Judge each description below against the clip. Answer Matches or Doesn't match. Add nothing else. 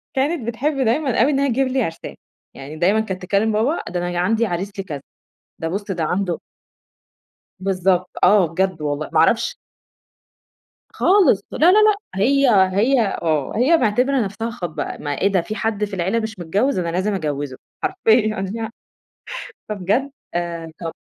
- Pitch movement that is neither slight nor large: Doesn't match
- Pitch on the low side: Doesn't match